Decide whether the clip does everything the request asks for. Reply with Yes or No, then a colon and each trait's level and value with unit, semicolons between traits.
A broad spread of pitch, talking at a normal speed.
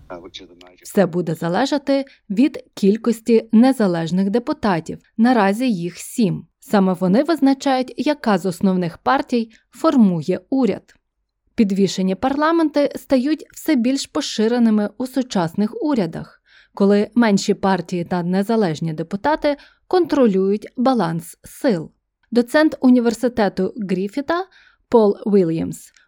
No: wide, 5.7 semitones; slow, 95 wpm